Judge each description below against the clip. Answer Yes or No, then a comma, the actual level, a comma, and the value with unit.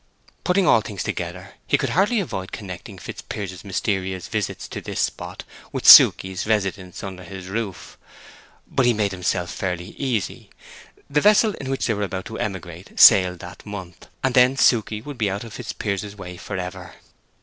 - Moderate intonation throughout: Yes, average, 3.7 semitones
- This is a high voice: No, low, 100 Hz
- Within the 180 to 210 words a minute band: No, average, 170 wpm